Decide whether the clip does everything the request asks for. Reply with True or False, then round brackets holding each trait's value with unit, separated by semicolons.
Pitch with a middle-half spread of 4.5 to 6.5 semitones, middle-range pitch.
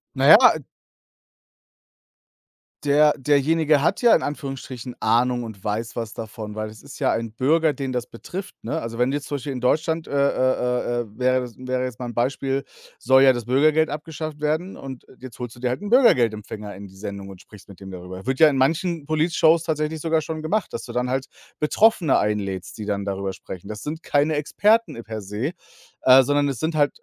False (5.1 semitones; 130 Hz)